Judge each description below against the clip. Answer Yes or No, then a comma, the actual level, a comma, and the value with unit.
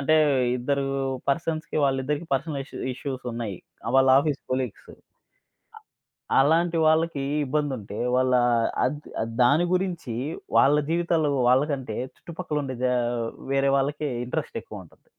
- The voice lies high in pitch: No, medium, 140 Hz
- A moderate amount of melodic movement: Yes, average, 3.4 semitones